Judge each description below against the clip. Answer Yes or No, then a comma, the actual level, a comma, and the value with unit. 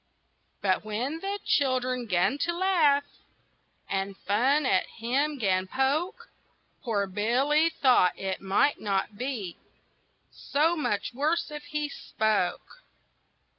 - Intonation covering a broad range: Yes, wide, 6.8 semitones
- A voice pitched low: No, very high, 255 Hz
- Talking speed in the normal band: No, slow, 115 wpm